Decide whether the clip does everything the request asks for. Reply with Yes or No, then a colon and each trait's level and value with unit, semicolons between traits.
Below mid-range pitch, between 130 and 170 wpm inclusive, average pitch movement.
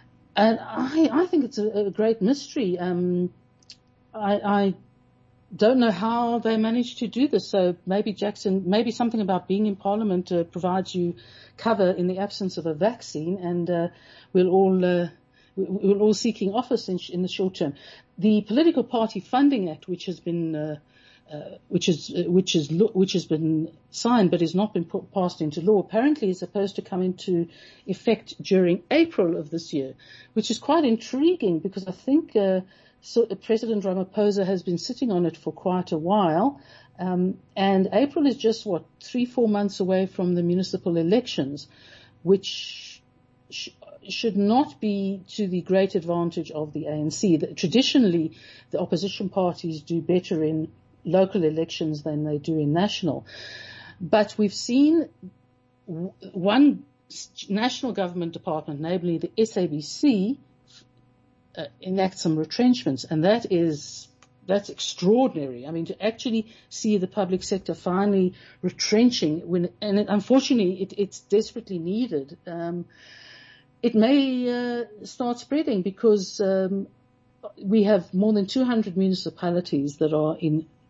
No: high, 190 Hz; average, 150 wpm; average, 4.3 semitones